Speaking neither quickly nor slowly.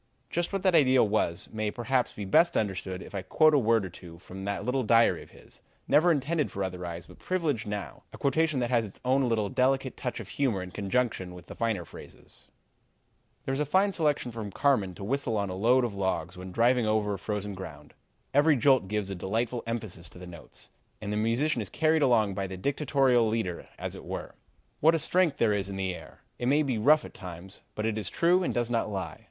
No: fast, 225 wpm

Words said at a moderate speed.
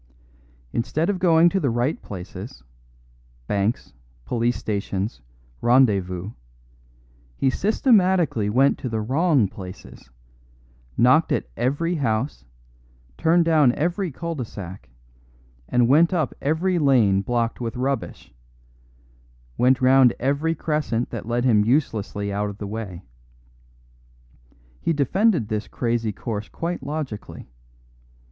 No: slow, 115 wpm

